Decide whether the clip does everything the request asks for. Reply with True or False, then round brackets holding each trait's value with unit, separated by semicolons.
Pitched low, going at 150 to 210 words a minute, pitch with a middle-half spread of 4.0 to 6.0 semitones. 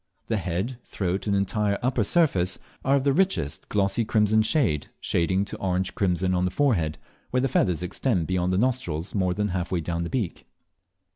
True (95 Hz; 190 wpm; 4.7 semitones)